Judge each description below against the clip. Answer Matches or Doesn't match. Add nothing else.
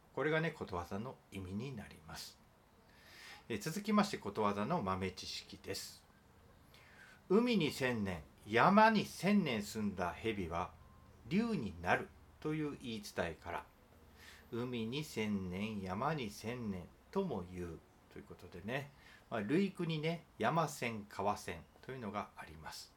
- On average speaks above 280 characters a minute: Doesn't match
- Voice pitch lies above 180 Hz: Doesn't match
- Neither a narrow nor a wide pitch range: Doesn't match